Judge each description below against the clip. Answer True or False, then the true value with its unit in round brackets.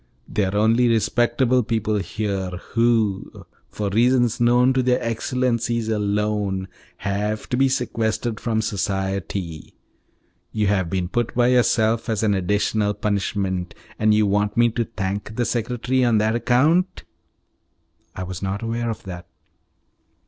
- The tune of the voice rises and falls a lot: False (3.0 semitones)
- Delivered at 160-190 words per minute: False (140 wpm)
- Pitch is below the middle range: True (110 Hz)